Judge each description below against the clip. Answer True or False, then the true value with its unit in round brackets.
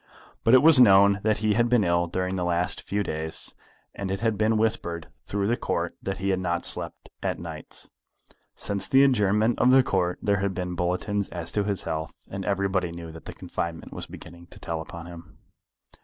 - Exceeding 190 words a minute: True (205 wpm)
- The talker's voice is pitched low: True (95 Hz)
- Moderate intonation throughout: True (3.4 semitones)